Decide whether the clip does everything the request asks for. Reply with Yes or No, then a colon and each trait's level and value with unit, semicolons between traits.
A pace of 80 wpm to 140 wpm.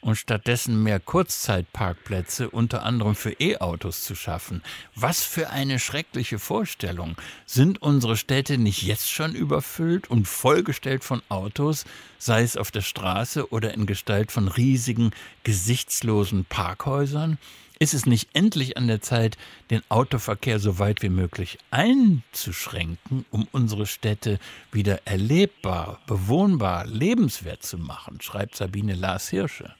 Yes: average, 130 wpm